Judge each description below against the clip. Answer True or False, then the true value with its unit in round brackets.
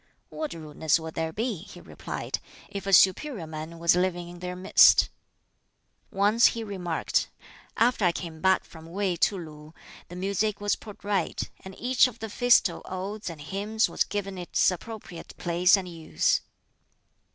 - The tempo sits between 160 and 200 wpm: True (165 wpm)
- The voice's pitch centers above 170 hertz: True (185 Hz)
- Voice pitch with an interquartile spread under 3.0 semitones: False (3.6 semitones)